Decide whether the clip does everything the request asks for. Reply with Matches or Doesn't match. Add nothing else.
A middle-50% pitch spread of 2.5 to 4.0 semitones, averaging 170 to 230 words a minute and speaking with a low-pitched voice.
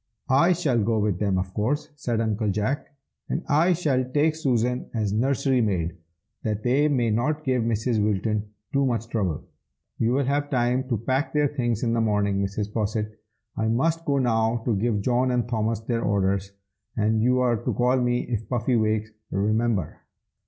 Matches